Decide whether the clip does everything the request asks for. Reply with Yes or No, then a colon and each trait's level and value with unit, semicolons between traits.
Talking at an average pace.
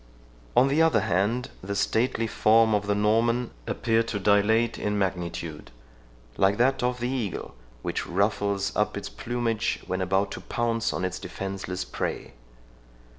Yes: average, 150 wpm